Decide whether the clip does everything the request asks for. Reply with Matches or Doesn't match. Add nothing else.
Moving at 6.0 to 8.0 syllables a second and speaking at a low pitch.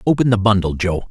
Matches